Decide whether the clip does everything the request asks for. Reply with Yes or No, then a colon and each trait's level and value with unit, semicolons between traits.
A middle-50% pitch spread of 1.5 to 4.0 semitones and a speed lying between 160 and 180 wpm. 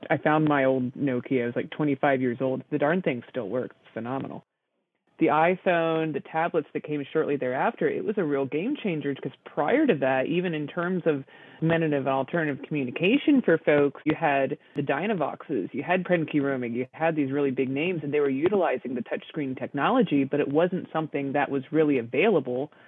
No: average, 2.9 semitones; average, 190 wpm